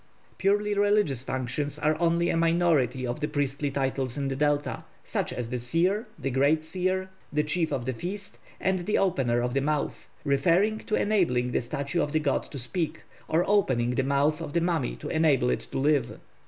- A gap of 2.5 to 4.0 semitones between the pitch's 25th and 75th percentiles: No, average, 4.6 semitones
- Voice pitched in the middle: Yes, medium, 150 Hz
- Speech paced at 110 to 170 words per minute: No, average, 195 wpm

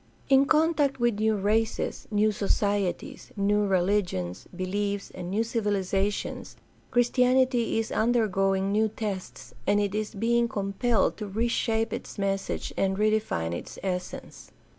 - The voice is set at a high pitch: Yes, high, 205 Hz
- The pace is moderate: No, slow, 125 wpm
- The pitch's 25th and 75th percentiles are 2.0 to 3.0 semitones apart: Yes, average, 2.7 semitones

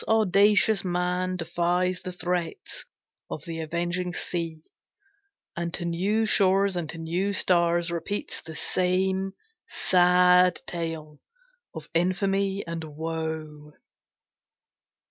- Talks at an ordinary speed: No, slow, 105 wpm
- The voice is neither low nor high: Yes, medium, 175 Hz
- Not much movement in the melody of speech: Yes, narrow, 2.0 semitones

